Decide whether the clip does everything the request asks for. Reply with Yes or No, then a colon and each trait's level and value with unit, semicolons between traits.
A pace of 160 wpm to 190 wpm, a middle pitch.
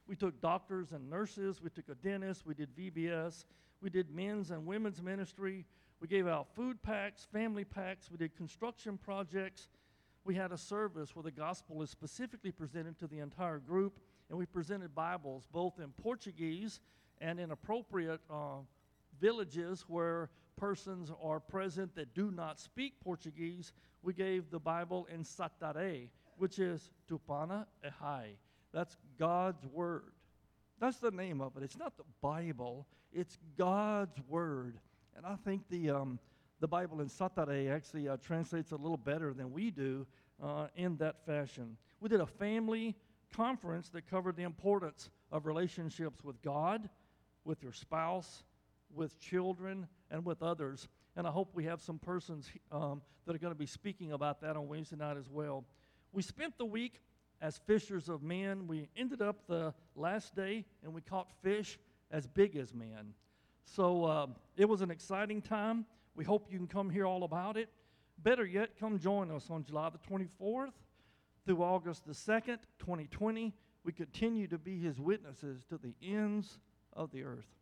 Yes: average, 170 wpm; medium, 170 Hz